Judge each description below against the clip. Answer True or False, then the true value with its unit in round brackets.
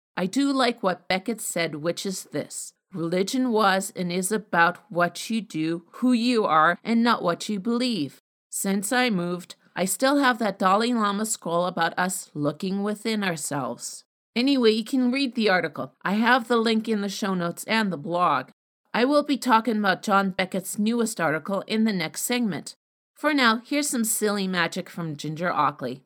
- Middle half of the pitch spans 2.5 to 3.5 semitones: False (4.6 semitones)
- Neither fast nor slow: True (180 wpm)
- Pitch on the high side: True (200 Hz)